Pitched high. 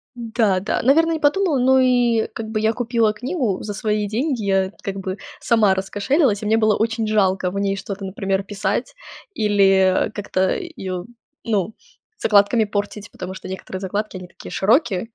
Yes: high, 210 Hz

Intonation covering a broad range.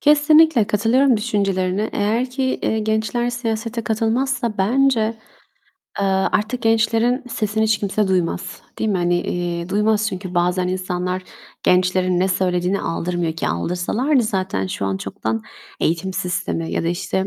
No: average, 4.0 semitones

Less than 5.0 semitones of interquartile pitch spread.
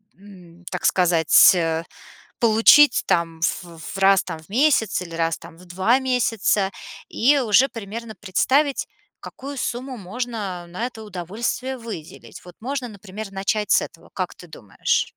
No: wide, 5.5 semitones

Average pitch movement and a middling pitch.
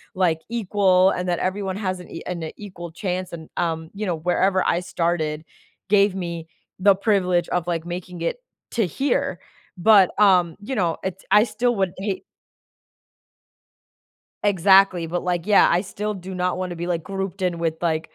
No: narrow, 2.3 semitones; medium, 180 Hz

